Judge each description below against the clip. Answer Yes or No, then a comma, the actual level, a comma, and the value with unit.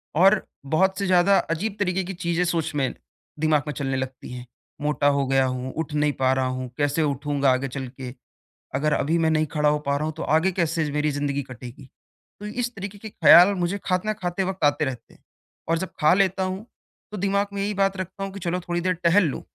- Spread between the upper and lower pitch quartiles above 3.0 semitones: Yes, average, 5.0 semitones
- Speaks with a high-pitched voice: No, medium, 160 Hz